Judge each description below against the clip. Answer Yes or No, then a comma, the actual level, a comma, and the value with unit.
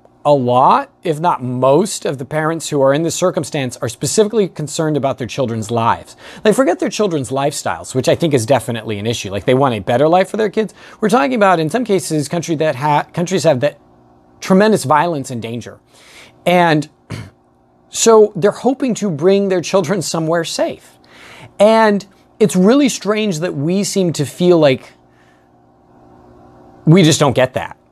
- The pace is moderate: Yes, average, 180 wpm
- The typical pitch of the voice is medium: Yes, medium, 150 Hz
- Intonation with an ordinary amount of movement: No, wide, 8.0 semitones